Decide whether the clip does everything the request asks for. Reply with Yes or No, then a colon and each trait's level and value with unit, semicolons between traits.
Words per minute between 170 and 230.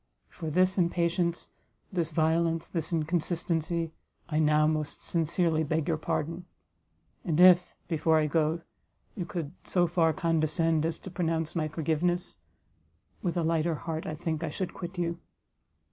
No: average, 145 wpm